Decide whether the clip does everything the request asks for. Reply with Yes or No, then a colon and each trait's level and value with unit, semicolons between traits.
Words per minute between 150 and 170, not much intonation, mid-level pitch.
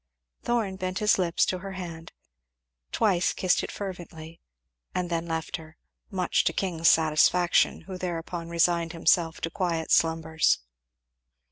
No: slow, 135 wpm; narrow, 2.0 semitones; medium, 170 Hz